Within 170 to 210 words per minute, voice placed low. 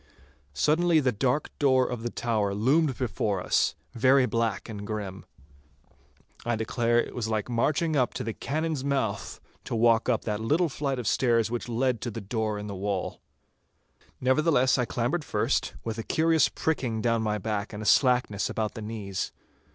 Yes: average, 175 wpm; low, 115 Hz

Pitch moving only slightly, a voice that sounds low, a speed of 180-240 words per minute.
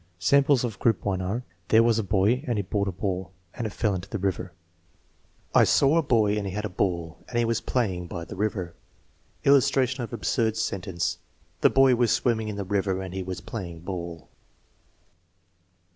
No: average, 4.0 semitones; low, 100 Hz; fast, 205 wpm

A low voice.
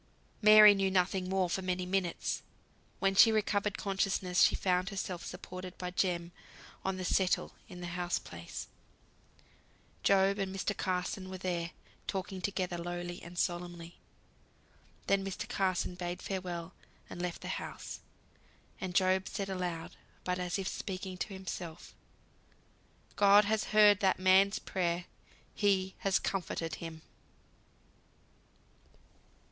No: medium, 185 Hz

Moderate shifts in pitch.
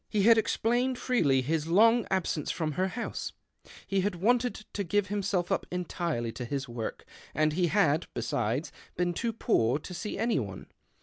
No: wide, 6.2 semitones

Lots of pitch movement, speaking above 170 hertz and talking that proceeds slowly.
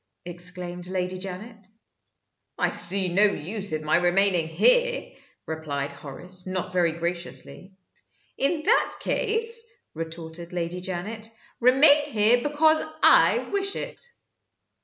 Yes: wide, 7.4 semitones; medium, 185 Hz; slow, 115 wpm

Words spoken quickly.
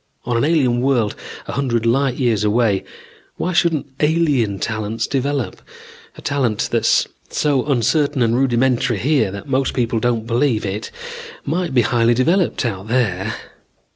No: average, 145 wpm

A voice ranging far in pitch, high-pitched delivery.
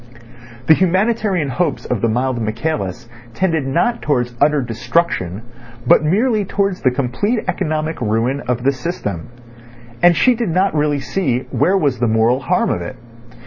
No: wide, 7.0 semitones; medium, 145 Hz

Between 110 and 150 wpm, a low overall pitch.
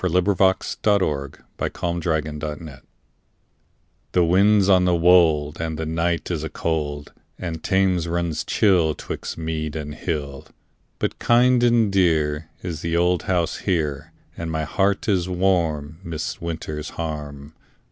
Yes: average, 145 wpm; very low, 85 Hz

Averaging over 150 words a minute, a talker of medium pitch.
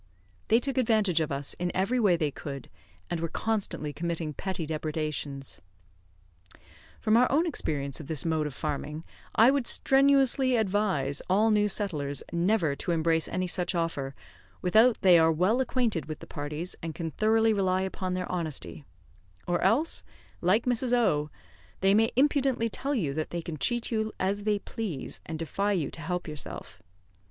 Yes: average, 170 wpm; medium, 180 Hz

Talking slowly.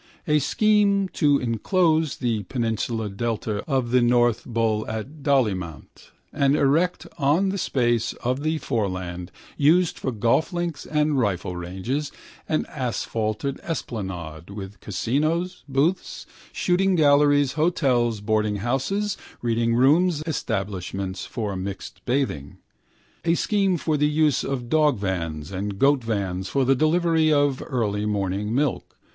Yes: slow, 120 wpm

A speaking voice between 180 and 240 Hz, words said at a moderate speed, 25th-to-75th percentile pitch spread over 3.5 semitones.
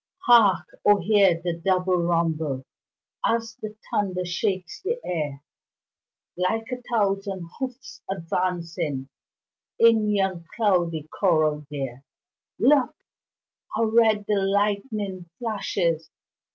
No: high, 190 Hz; slow, 100 wpm; average, 4.2 semitones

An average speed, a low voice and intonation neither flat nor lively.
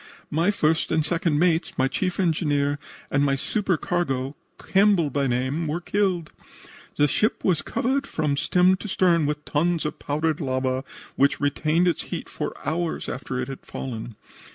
No: average, 160 wpm; medium, 155 Hz; average, 3.8 semitones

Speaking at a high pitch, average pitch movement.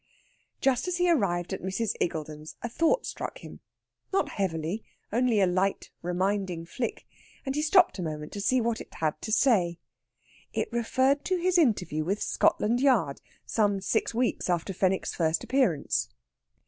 No: high, 205 Hz; wide, 6.7 semitones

